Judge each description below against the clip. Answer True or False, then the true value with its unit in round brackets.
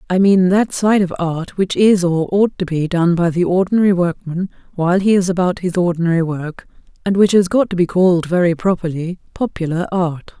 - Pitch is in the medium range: True (180 Hz)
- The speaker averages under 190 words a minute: False (200 wpm)